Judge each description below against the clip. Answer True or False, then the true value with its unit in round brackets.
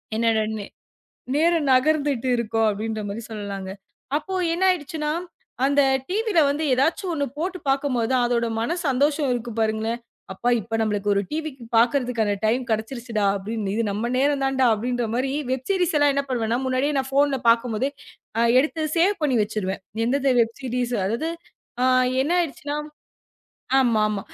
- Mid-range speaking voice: False (255 Hz)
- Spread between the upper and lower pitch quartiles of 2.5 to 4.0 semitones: False (4.4 semitones)